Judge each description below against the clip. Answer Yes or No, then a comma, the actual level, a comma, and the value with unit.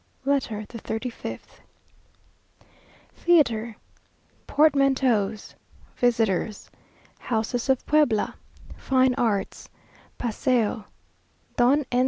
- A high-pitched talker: Yes, high, 245 Hz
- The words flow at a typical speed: No, slow, 75 wpm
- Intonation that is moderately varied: Yes, average, 3.5 semitones